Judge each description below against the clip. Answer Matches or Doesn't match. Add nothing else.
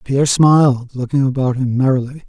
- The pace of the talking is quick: Doesn't match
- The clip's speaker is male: Matches